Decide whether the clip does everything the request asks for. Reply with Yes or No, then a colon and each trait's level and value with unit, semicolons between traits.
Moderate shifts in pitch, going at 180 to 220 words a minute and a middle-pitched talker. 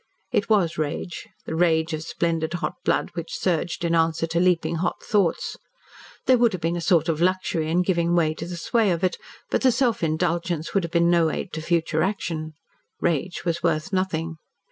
No: narrow, 2.0 semitones; average, 200 wpm; medium, 170 Hz